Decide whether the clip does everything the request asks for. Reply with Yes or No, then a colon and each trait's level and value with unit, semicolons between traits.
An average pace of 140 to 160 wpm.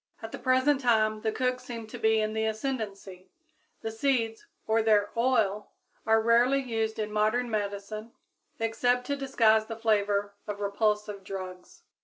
Yes: average, 155 wpm